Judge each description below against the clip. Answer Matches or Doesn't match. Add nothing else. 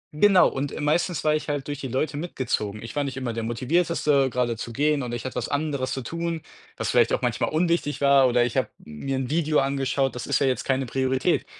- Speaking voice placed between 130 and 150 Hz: Matches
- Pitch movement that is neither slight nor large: Matches